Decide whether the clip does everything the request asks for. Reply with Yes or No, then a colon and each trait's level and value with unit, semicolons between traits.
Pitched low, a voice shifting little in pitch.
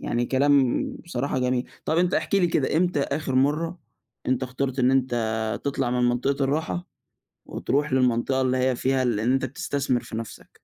Yes: low, 130 Hz; narrow, 2.3 semitones